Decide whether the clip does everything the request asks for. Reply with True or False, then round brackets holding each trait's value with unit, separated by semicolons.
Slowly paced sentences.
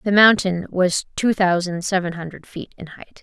False (185 wpm)